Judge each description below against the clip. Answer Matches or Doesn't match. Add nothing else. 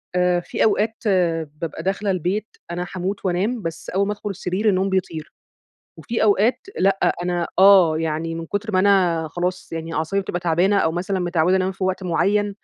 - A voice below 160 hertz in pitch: Doesn't match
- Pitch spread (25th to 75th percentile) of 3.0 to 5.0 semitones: Doesn't match